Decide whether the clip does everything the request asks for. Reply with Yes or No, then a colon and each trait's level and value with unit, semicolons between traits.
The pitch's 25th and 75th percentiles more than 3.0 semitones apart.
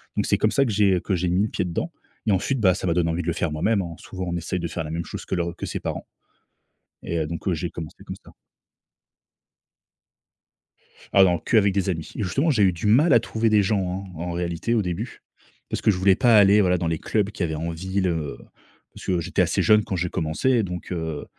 Yes: average, 3.5 semitones